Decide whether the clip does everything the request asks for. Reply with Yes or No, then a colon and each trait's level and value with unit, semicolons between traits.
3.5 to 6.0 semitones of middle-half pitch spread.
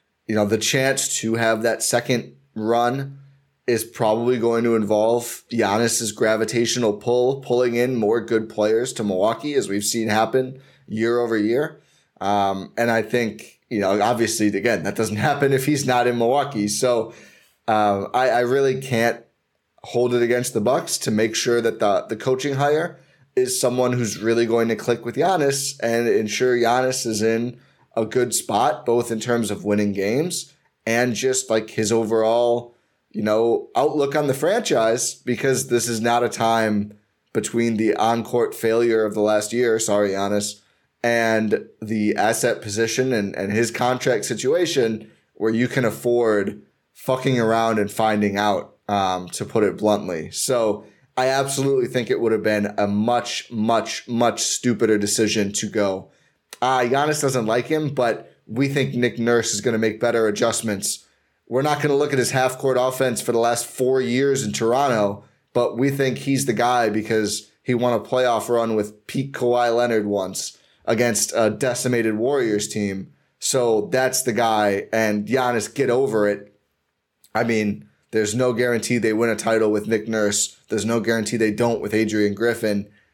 No: narrow, 2.5 semitones